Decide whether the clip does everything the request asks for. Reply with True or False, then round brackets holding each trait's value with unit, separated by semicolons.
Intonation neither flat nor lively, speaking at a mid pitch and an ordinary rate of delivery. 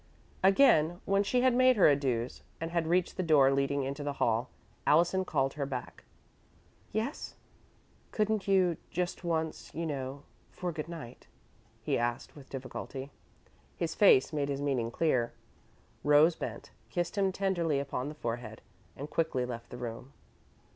True (4.8 semitones; 150 Hz; 155 wpm)